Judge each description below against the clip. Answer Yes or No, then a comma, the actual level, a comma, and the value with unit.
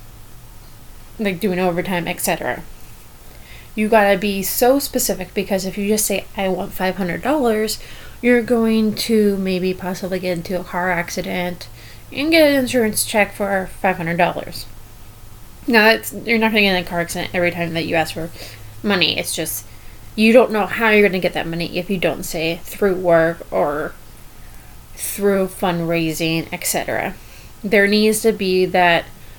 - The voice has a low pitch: No, medium, 185 Hz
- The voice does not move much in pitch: No, average, 3.9 semitones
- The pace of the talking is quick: No, average, 170 wpm